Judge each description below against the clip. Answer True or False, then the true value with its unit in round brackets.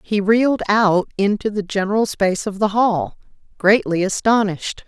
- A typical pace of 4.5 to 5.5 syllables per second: True (5.0 syllables/s)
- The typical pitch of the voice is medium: False (205 Hz)